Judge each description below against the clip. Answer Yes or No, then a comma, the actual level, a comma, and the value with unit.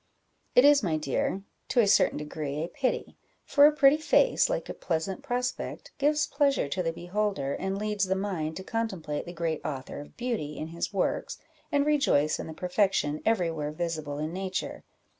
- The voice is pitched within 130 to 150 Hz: No, high, 190 Hz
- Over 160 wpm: Yes, average, 185 wpm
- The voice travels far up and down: Yes, wide, 7.9 semitones